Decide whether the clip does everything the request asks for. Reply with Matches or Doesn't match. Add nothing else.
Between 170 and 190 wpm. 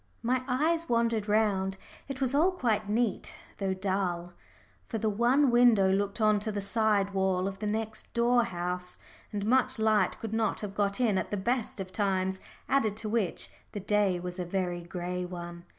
Matches